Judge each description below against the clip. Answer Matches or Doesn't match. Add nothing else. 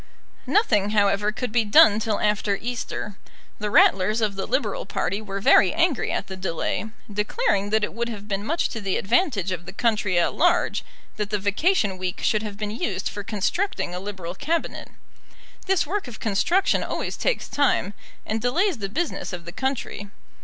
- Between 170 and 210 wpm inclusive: Matches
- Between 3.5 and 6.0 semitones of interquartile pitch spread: Matches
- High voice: Matches